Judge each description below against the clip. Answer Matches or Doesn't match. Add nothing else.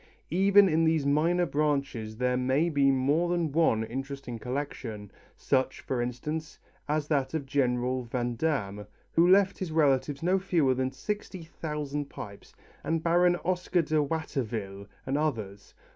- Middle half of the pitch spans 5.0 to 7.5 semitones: Doesn't match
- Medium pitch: Matches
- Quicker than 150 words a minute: Doesn't match